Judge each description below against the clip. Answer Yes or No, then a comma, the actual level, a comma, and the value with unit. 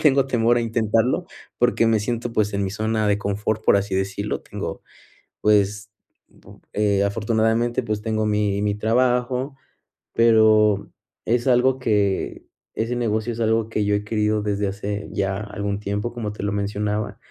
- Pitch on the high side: No, low, 110 Hz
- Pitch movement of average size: No, narrow, 2.1 semitones